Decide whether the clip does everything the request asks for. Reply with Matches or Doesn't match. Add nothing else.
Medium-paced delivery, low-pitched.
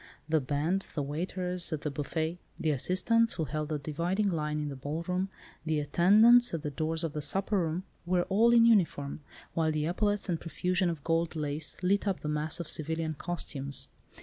Doesn't match